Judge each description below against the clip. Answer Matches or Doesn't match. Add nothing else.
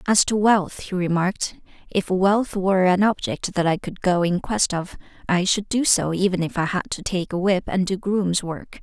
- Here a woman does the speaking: Matches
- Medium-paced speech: Doesn't match